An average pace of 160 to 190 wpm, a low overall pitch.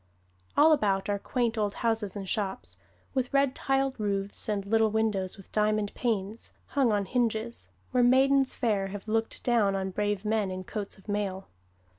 No: average, 170 wpm; high, 215 Hz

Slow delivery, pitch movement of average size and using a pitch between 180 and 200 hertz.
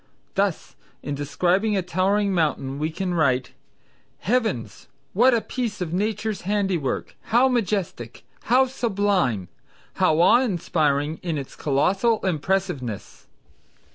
No: slow, 115 wpm; wide, 6.0 semitones; medium, 185 Hz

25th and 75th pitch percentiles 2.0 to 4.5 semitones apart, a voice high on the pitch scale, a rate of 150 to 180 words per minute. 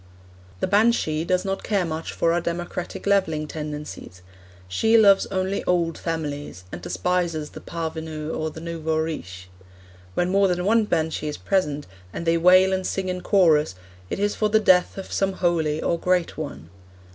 No: average, 3.4 semitones; medium, 170 Hz; average, 170 wpm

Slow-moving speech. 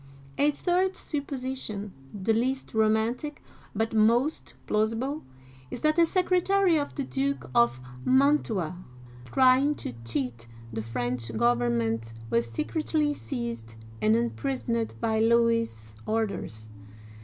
Yes: slow, 120 wpm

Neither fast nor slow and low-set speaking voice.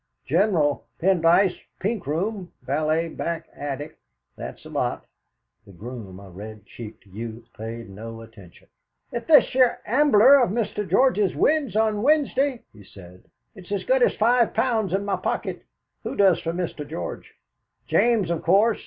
No: average, 155 wpm; medium, 180 Hz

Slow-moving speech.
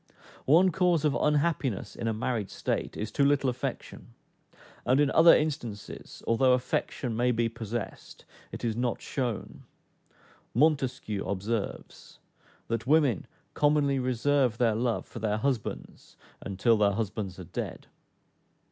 Yes: slow, 130 wpm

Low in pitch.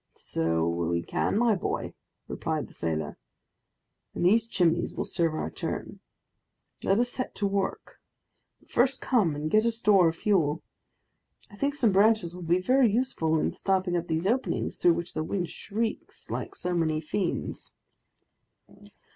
No: medium, 185 Hz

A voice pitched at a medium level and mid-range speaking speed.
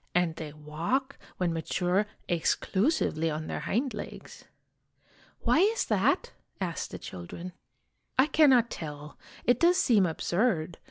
No: medium, 180 Hz; slow, 130 wpm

